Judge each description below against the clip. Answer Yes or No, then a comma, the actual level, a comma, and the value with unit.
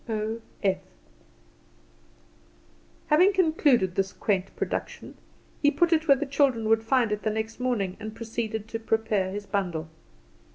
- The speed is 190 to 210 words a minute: No, slow, 135 wpm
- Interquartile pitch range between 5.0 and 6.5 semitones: No, average, 4.6 semitones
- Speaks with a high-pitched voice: Yes, high, 225 Hz